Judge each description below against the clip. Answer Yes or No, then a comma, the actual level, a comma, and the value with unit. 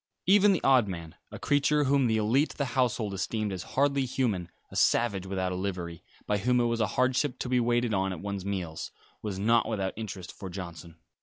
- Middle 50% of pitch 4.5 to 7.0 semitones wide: Yes, average, 5.0 semitones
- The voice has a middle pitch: No, low, 110 Hz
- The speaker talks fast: Yes, fast, 215 wpm